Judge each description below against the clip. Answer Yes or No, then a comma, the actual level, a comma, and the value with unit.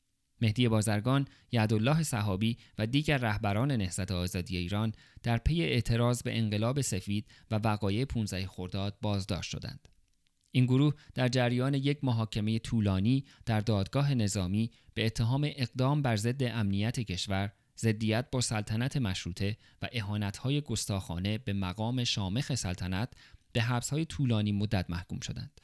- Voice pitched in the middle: No, low, 110 Hz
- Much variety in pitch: No, average, 3.6 semitones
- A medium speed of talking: Yes, average, 130 wpm